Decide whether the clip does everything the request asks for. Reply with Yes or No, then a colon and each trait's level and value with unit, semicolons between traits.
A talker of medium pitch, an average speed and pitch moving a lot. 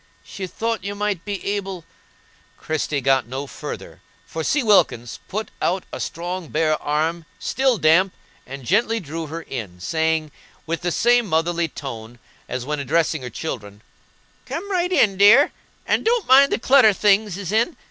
Yes: medium, 170 Hz; average, 165 wpm; wide, 5.8 semitones